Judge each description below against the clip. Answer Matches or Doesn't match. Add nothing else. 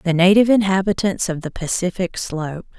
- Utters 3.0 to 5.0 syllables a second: Doesn't match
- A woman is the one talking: Matches